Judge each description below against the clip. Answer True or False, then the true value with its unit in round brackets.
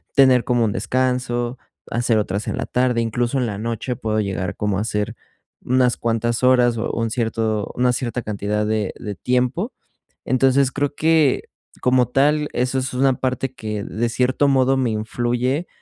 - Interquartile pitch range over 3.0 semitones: False (2.7 semitones)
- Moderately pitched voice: False (120 Hz)